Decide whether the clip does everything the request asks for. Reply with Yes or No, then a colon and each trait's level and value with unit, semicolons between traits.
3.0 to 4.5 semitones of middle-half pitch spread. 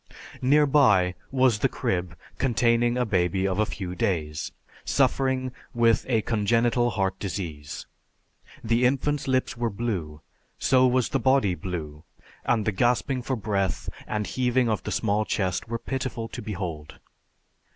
No: average, 4.9 semitones